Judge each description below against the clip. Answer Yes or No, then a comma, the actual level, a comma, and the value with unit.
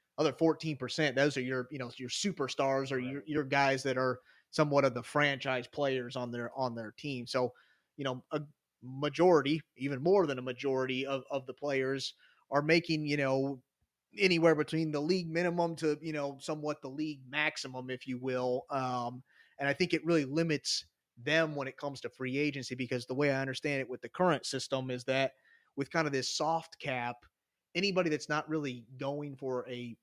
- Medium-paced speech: Yes, average, 195 wpm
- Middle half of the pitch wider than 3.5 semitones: No, average, 2.8 semitones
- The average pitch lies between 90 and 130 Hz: No, medium, 140 Hz